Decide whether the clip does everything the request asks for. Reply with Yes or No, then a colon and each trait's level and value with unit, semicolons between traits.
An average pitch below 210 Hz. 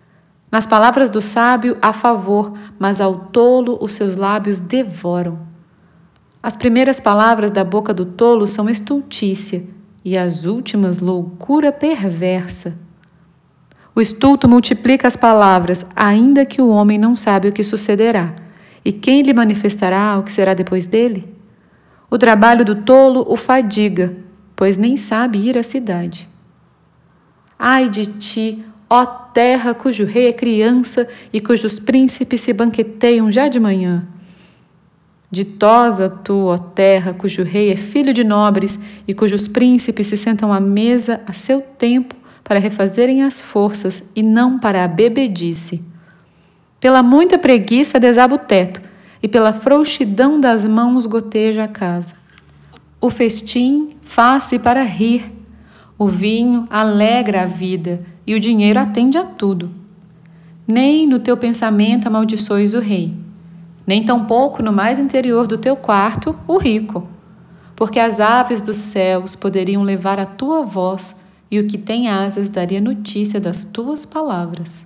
No: high, 215 Hz